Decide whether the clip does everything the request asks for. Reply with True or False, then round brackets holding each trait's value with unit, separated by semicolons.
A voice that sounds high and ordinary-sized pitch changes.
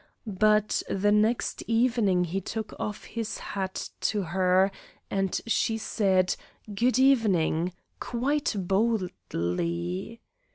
True (200 Hz; 3.6 semitones)